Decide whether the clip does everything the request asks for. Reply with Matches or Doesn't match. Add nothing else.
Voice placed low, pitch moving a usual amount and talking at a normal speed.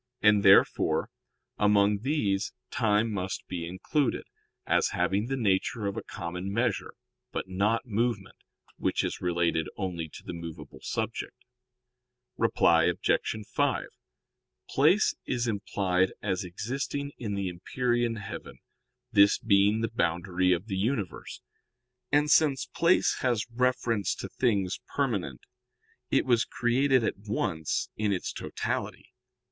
Doesn't match